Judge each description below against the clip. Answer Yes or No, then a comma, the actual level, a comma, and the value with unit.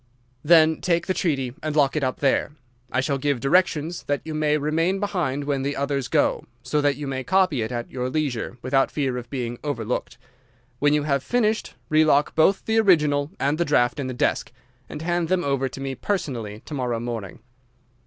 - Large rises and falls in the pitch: No, average, 3.3 semitones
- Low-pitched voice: No, medium, 145 Hz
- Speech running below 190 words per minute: No, average, 200 wpm